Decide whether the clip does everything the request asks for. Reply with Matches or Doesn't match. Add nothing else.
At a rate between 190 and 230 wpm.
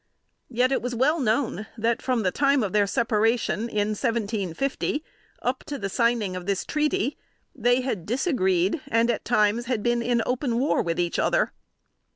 Doesn't match